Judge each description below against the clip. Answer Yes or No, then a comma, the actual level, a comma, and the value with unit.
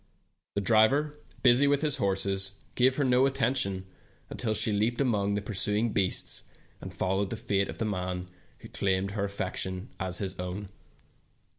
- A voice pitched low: Yes, low, 100 Hz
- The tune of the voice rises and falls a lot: No, average, 4.0 semitones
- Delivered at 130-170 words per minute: Yes, average, 160 wpm